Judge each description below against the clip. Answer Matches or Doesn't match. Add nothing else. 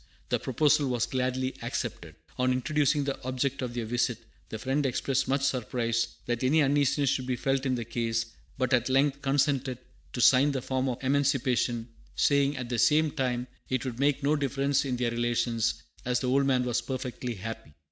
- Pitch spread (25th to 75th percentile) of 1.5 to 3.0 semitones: Matches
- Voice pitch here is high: Doesn't match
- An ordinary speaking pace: Matches